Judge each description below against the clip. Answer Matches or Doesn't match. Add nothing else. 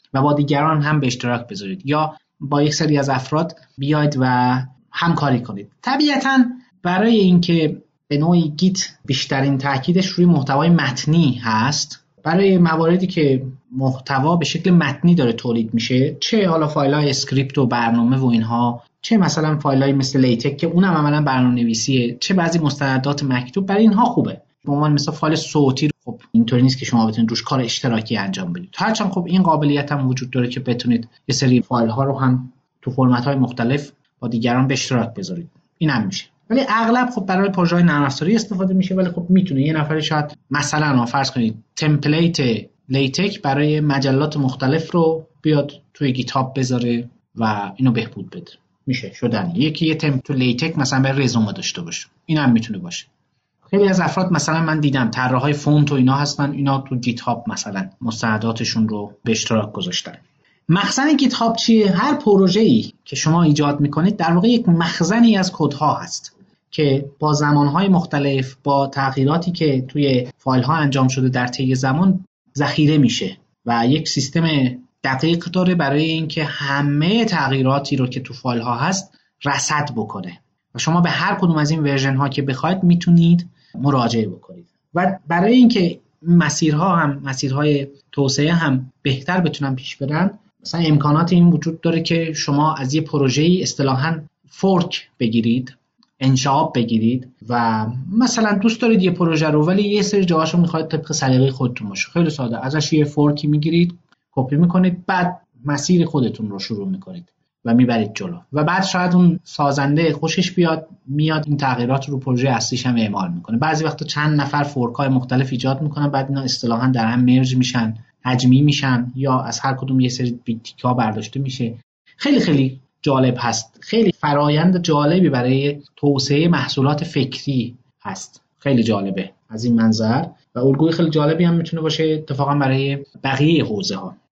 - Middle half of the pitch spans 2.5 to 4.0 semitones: Doesn't match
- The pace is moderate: Doesn't match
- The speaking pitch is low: Doesn't match